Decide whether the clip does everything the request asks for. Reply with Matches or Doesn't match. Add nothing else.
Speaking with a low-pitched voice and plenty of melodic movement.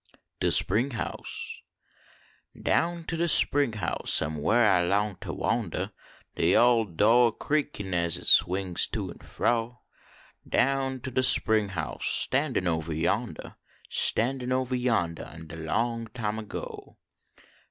Matches